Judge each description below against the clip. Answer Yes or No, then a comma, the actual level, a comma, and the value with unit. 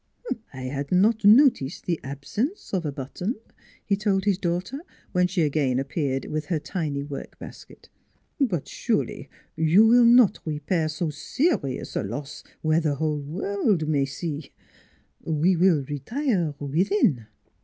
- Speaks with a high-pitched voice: No, medium, 160 Hz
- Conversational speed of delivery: Yes, average, 155 wpm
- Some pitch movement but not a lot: No, wide, 5.7 semitones